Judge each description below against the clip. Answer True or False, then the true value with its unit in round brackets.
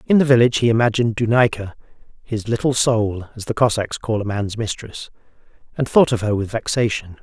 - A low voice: True (115 Hz)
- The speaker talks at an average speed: True (185 wpm)